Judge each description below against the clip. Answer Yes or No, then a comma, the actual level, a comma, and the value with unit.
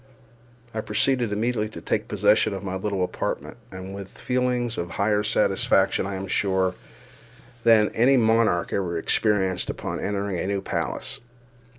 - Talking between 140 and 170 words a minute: Yes, average, 155 wpm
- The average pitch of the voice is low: Yes, low, 100 Hz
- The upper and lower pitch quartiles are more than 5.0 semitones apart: No, average, 2.8 semitones